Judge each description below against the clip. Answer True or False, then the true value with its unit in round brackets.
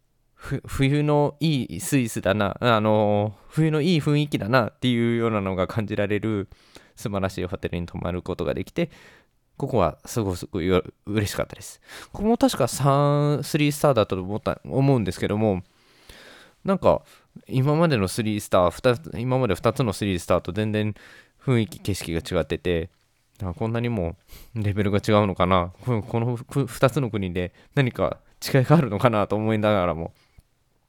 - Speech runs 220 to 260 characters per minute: False (330 characters per minute)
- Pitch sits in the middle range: False (110 Hz)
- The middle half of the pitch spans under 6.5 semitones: True (5.6 semitones)